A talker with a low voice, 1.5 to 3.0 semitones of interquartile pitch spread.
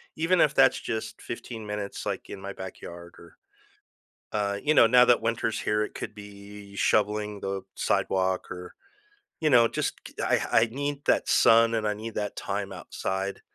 Yes: low, 105 Hz; narrow, 2.6 semitones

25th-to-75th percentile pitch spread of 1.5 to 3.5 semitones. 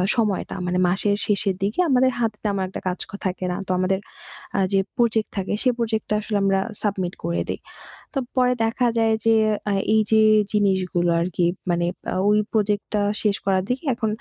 Yes: average, 3.0 semitones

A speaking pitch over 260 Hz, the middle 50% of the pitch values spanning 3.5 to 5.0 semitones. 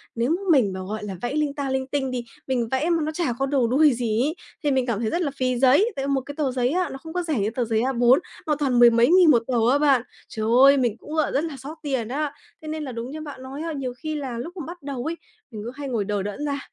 Yes: very high, 270 Hz; average, 3.9 semitones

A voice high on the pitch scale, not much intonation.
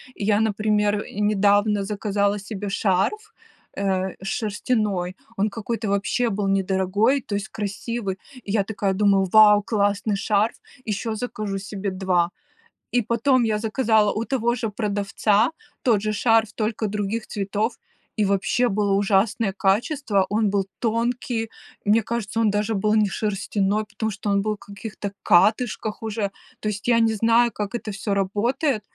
Yes: high, 210 Hz; narrow, 2.0 semitones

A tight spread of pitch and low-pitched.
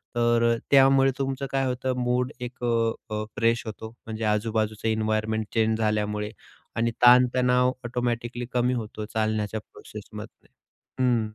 Yes: narrow, 2.3 semitones; low, 115 Hz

